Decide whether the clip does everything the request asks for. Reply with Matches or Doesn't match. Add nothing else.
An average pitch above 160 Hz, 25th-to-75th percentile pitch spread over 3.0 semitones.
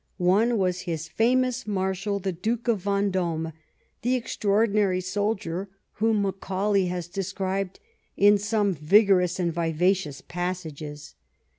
Doesn't match